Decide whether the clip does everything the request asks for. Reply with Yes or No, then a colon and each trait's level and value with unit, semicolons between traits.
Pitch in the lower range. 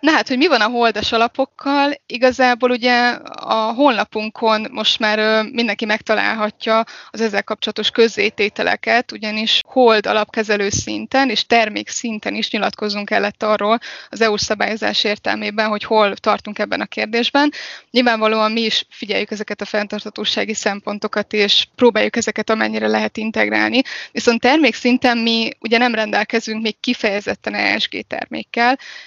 No: high, 220 Hz